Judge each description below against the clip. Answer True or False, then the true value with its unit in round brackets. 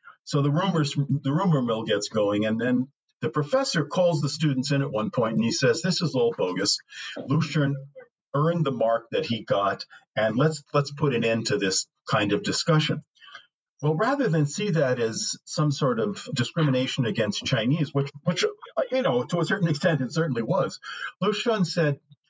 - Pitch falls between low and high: True (150 Hz)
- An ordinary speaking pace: True (190 wpm)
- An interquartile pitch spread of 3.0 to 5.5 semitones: True (3.9 semitones)